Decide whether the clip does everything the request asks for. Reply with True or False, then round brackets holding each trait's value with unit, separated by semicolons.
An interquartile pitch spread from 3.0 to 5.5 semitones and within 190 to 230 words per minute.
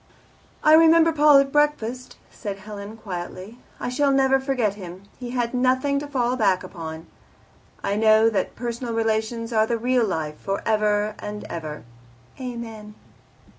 False (3.8 semitones; 150 wpm)